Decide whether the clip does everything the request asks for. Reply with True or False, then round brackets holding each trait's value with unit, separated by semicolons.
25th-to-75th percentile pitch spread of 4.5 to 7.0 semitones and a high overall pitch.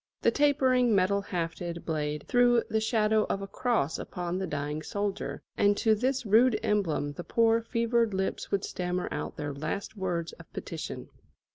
True (5.1 semitones; 200 Hz)